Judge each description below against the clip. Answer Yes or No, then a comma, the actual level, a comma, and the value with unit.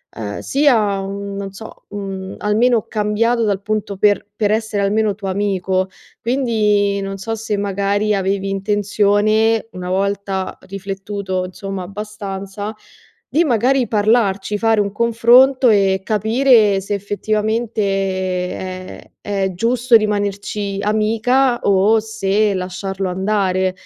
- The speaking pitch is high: Yes, high, 205 Hz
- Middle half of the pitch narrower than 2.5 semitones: Yes, narrow, 2.1 semitones